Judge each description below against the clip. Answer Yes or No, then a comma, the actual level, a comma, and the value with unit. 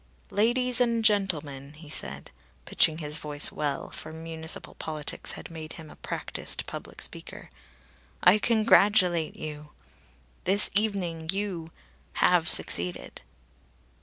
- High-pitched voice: No, medium, 165 Hz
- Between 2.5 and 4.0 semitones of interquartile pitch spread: No, average, 5.1 semitones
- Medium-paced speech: No, slow, 115 wpm